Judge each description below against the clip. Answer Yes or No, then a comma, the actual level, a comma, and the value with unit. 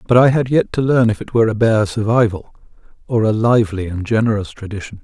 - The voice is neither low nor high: No, low, 110 Hz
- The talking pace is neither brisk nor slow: No, fast, 215 wpm